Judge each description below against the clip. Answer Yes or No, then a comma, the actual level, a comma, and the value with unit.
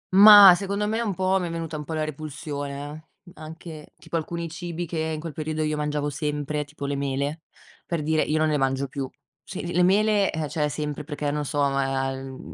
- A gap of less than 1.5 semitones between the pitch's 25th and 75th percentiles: No, average, 2.7 semitones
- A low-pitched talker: No, medium, 155 Hz